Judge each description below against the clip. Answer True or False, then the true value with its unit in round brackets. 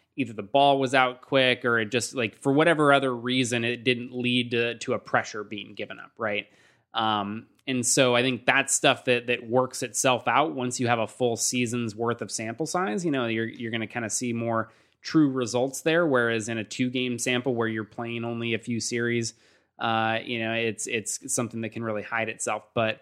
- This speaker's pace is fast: True (220 wpm)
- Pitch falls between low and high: False (120 Hz)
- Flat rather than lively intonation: True (2.1 semitones)